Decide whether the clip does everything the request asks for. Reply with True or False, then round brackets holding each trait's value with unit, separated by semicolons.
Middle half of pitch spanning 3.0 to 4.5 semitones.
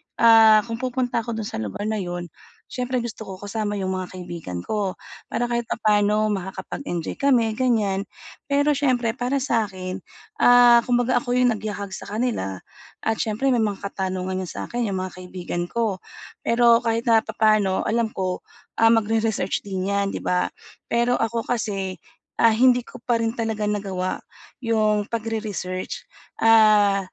True (3.4 semitones)